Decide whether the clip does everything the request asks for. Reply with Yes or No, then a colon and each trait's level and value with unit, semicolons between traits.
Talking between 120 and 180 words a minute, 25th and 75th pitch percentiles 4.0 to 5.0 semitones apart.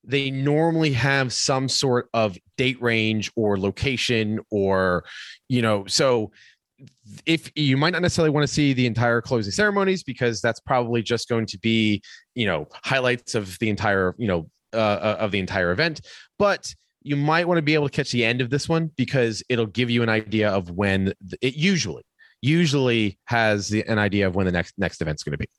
No: average, 195 wpm; average, 4.7 semitones